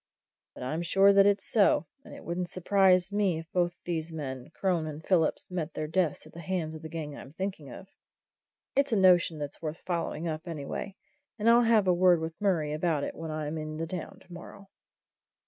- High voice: No, medium, 170 Hz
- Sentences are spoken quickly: Yes, fast, 210 wpm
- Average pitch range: Yes, average, 3.2 semitones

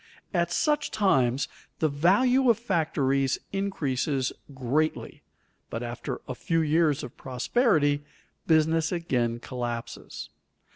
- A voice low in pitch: No, medium, 155 Hz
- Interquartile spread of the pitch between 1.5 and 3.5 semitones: No, average, 5.0 semitones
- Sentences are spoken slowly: Yes, slow, 105 wpm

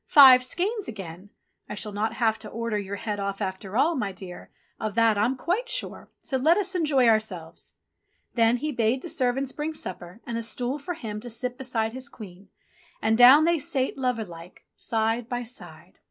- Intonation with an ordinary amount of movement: Yes, average, 4.0 semitones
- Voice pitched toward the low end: No, high, 230 Hz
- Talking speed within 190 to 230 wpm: Yes, average, 195 wpm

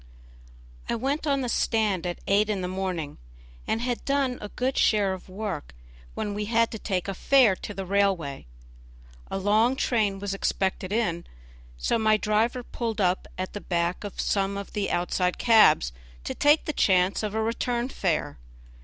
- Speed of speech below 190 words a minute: Yes, average, 180 wpm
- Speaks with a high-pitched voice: Yes, high, 205 Hz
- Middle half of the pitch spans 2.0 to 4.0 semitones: Yes, average, 3.6 semitones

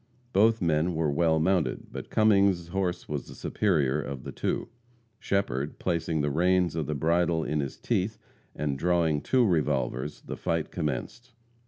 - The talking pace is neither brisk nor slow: Yes, average, 165 wpm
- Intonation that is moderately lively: Yes, average, 3.7 semitones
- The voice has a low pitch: Yes, very low, 80 Hz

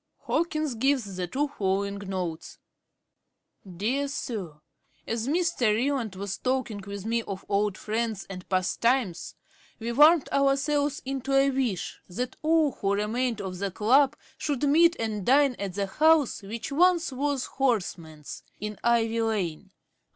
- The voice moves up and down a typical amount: No, wide, 5.7 semitones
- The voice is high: Yes, high, 230 Hz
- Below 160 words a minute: Yes, average, 150 wpm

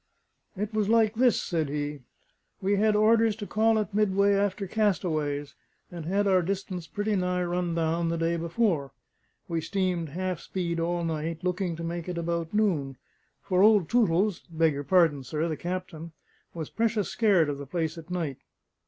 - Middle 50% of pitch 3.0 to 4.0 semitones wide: Yes, average, 3.7 semitones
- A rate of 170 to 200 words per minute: Yes, average, 175 wpm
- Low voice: No, medium, 175 Hz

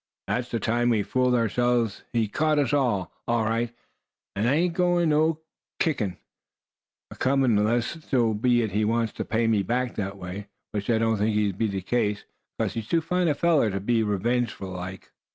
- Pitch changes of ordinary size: Yes, average, 3.6 semitones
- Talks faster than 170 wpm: Yes, average, 190 wpm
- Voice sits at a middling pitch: No, low, 115 Hz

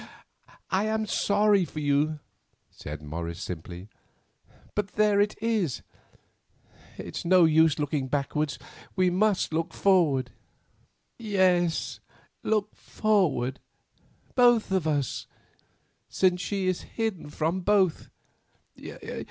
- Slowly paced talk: Yes, slow, 105 wpm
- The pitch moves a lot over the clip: Yes, wide, 5.7 semitones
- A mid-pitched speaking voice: Yes, medium, 180 Hz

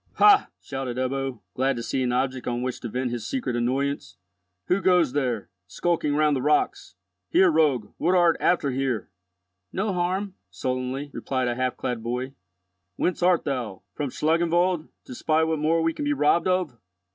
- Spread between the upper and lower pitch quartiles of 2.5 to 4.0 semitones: No, average, 5.2 semitones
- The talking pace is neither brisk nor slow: Yes, average, 175 wpm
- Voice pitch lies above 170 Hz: No, medium, 140 Hz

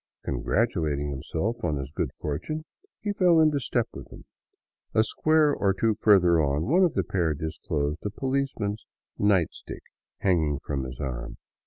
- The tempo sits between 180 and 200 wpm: No, average, 170 wpm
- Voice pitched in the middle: No, very low, 95 Hz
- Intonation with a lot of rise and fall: Yes, wide, 8.6 semitones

